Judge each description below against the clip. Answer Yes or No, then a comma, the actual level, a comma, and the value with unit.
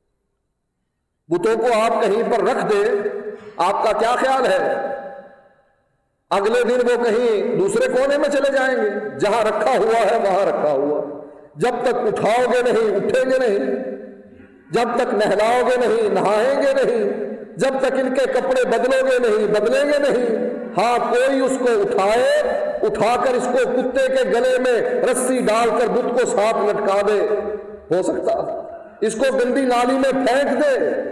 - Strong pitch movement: Yes, wide, 5.9 semitones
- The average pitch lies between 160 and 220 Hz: No, very high, 260 Hz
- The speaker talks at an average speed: Yes, average, 165 wpm